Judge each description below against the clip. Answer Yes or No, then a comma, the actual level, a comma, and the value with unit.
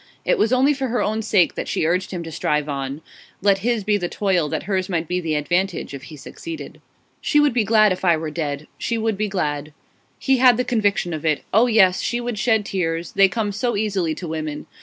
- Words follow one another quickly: Yes, fast, 235 wpm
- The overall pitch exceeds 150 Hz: Yes, high, 190 Hz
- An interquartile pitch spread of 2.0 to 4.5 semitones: No, wide, 5.5 semitones